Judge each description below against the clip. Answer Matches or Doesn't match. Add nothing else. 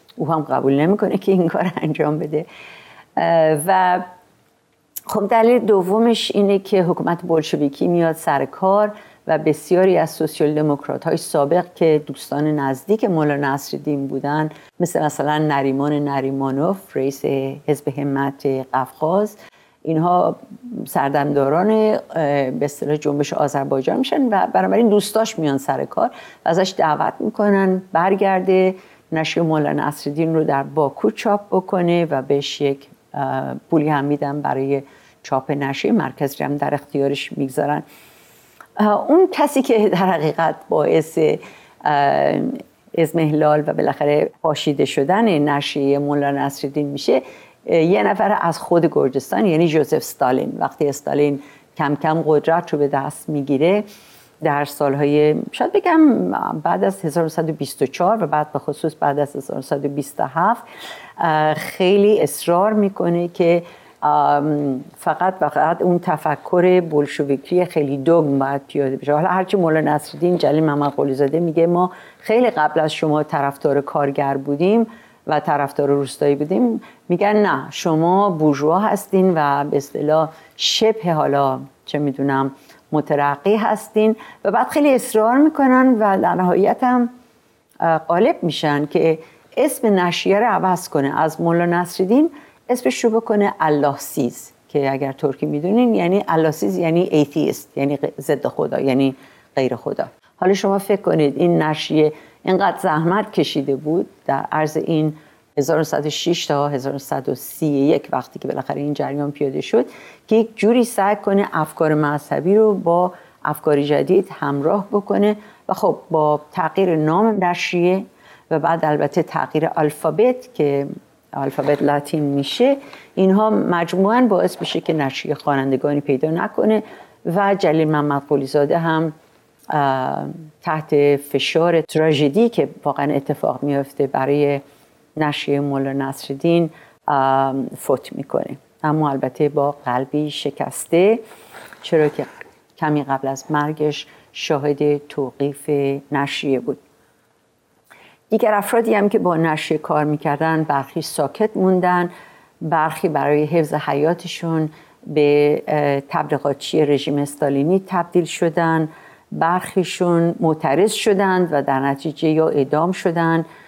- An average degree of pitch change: Matches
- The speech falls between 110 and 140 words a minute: Matches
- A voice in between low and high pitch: Matches